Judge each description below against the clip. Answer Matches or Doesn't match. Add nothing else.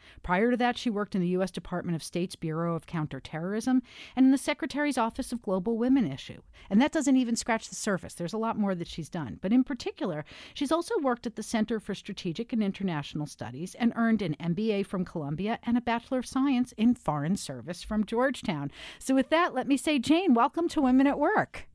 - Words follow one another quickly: Matches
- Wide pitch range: Matches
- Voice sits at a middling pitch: Doesn't match